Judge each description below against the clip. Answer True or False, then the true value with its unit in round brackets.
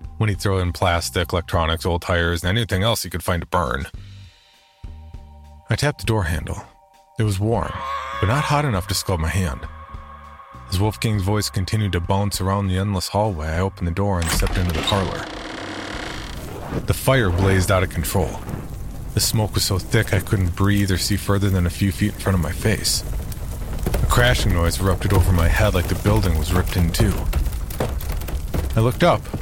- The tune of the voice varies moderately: True (3.8 semitones)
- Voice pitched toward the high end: False (95 Hz)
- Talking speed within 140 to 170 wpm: False (190 wpm)